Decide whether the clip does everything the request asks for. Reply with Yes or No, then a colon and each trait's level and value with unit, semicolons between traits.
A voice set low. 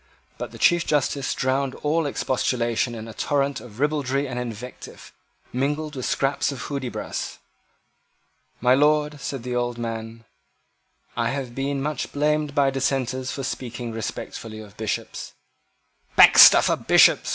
Yes: low, 130 Hz